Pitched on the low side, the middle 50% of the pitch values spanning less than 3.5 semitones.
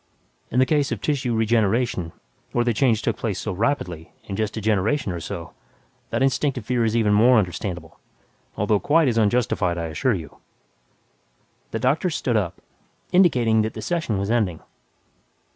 No: low, 110 Hz; average, 4.3 semitones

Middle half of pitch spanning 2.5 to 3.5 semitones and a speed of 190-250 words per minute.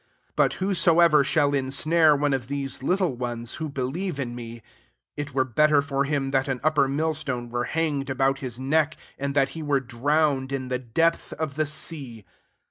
Yes: average, 2.9 semitones; average, 195 wpm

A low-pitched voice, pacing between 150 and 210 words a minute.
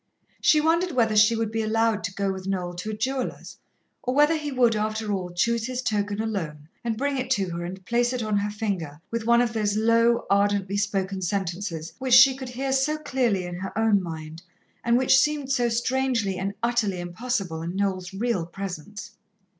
No: high, 215 Hz; average, 200 wpm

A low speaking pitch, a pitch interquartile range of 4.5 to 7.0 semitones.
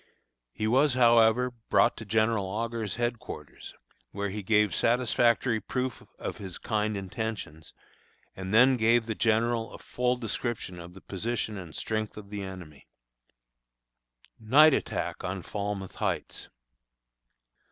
No: low, 110 Hz; average, 2.9 semitones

